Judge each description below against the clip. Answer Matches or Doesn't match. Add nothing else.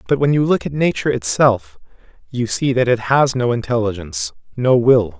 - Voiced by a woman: Doesn't match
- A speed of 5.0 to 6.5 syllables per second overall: Matches